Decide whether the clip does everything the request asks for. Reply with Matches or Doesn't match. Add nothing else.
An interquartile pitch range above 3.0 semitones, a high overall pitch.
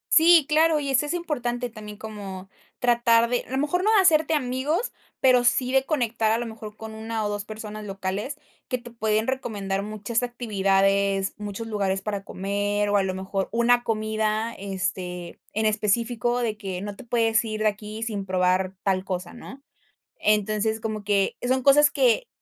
Matches